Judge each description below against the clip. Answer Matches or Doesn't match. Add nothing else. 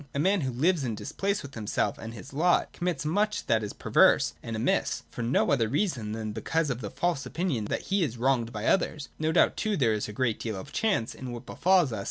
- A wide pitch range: Matches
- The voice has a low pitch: Matches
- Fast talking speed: Matches